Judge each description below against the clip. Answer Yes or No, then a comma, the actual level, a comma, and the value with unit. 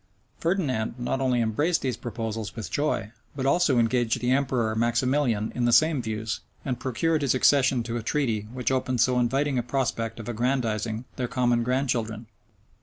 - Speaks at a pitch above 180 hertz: No, low, 125 Hz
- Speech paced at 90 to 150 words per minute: No, average, 170 wpm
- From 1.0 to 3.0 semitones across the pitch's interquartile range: Yes, average, 2.7 semitones